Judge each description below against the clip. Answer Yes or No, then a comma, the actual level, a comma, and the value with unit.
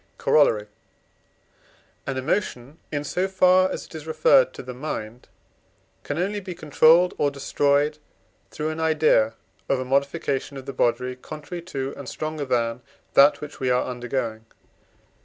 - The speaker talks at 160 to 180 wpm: No, average, 150 wpm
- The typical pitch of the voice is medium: Yes, medium, 145 Hz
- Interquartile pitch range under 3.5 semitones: No, average, 3.8 semitones